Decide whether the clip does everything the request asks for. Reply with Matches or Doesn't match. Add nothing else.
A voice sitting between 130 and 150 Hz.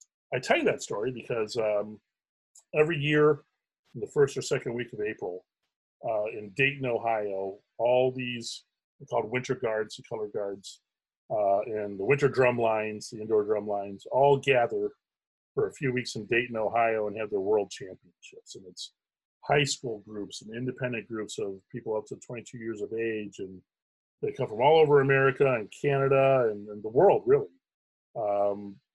Doesn't match